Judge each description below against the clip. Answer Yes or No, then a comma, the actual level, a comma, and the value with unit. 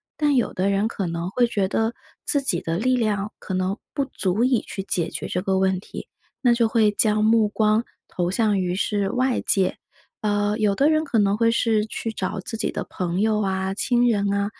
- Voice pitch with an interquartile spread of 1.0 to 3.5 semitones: Yes, average, 3.1 semitones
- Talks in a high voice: Yes, high, 210 Hz